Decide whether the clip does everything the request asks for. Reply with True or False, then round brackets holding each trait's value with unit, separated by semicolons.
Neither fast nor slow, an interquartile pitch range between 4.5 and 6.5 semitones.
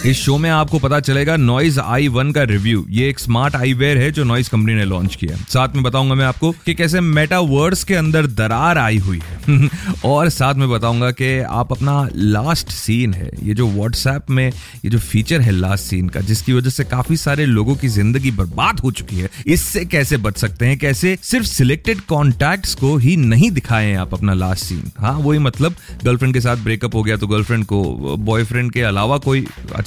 False (205 wpm; 4.8 semitones)